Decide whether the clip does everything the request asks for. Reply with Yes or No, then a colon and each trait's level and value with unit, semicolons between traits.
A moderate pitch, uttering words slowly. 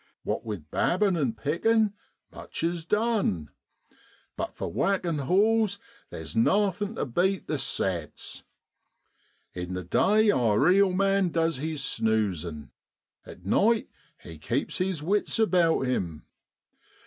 Yes: medium, 165 Hz; slow, 125 wpm